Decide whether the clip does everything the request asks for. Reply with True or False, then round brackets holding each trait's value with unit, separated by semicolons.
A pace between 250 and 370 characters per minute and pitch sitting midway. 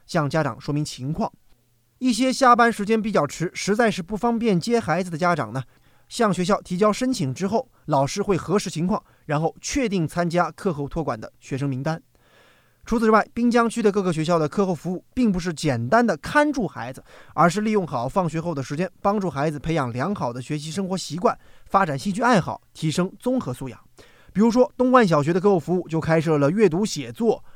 True (315 characters per minute; 180 Hz)